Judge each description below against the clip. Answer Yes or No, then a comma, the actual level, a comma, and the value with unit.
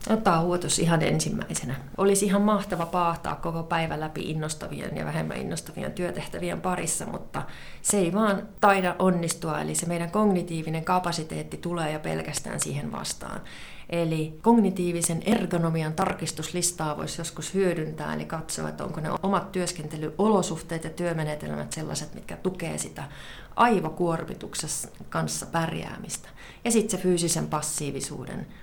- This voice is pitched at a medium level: Yes, medium, 170 Hz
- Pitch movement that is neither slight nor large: Yes, average, 3.2 semitones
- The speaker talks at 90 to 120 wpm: No, average, 130 wpm